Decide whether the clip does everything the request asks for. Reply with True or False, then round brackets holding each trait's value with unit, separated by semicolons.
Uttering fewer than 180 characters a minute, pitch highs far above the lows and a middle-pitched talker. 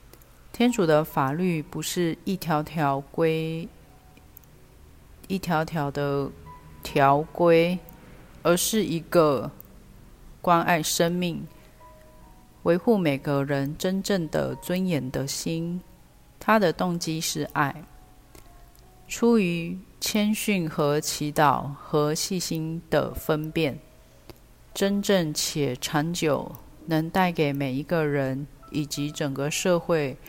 False (145 characters per minute; 3.7 semitones; 155 Hz)